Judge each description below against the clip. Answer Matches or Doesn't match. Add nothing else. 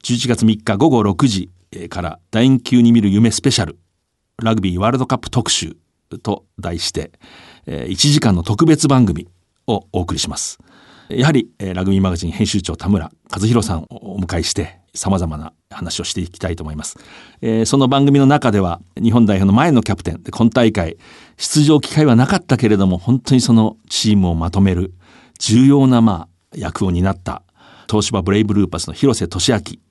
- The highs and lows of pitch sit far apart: Doesn't match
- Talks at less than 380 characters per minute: Matches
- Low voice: Matches